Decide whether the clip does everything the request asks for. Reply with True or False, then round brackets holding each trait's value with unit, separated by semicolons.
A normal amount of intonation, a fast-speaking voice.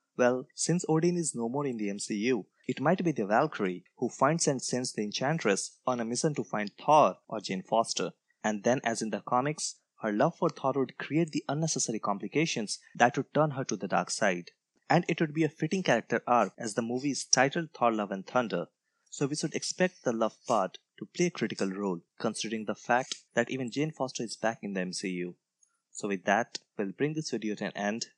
False (5.9 semitones; 220 wpm)